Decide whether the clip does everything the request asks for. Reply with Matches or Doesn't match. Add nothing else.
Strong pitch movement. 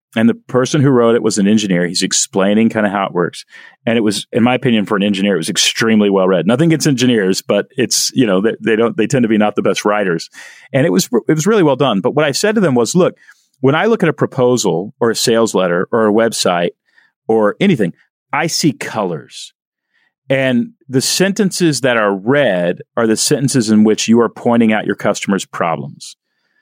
Doesn't match